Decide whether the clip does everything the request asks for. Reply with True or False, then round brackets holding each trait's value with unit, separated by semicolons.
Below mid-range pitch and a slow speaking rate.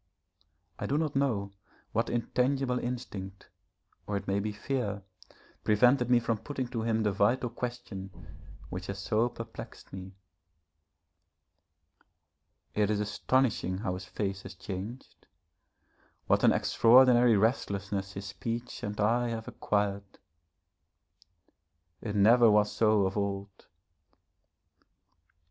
True (105 Hz; 120 wpm)